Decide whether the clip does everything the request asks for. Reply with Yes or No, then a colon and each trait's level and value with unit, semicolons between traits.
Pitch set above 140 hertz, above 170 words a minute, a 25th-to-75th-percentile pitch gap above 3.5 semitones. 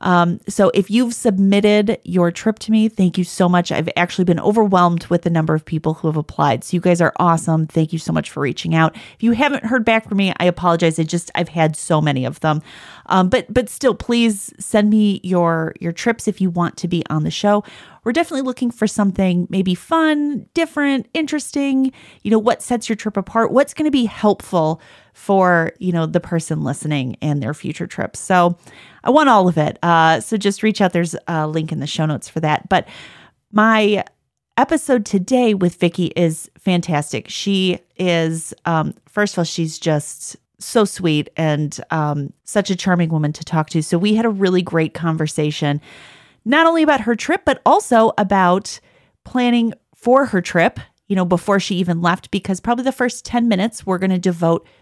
Yes: medium, 185 Hz; average, 200 wpm; average, 5.3 semitones